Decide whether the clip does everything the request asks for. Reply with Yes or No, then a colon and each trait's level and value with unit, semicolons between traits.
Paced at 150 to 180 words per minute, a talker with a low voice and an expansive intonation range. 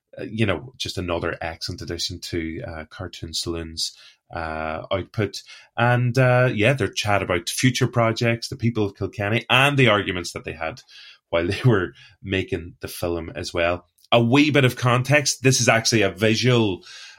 Yes: average, 170 wpm; low, 105 Hz; wide, 5.7 semitones